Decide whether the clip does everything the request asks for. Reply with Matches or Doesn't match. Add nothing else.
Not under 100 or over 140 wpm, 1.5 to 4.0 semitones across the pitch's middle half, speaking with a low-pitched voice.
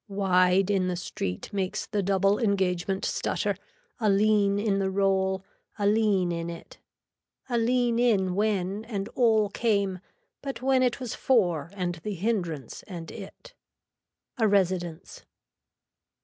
Doesn't match